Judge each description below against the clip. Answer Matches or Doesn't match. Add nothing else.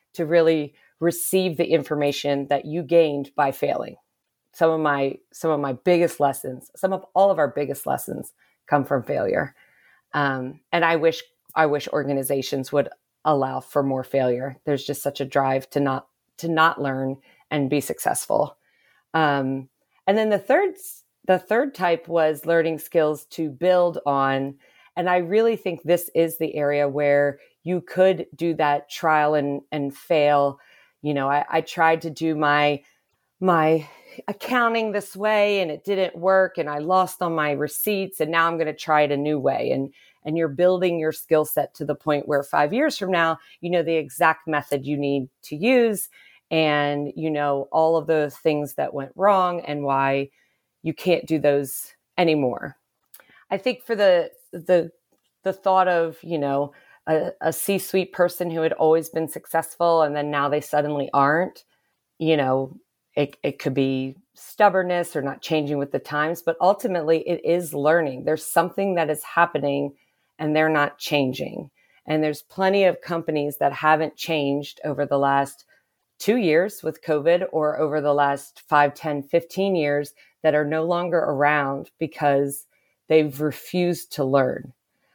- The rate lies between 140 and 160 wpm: Doesn't match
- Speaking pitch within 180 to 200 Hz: Doesn't match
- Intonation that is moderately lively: Matches